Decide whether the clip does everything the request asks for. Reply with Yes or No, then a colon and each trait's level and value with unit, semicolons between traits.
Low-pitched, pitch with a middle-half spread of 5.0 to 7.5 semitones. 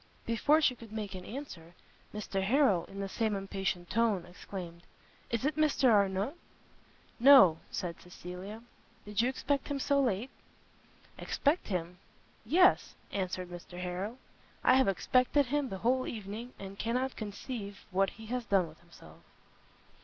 No: high, 210 Hz; wide, 5.4 semitones